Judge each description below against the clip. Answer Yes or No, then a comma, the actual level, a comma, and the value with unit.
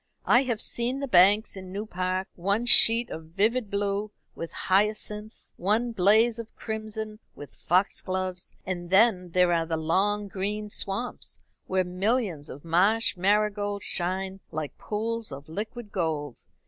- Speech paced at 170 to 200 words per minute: No, average, 145 wpm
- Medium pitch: No, high, 200 Hz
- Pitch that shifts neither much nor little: Yes, average, 3.2 semitones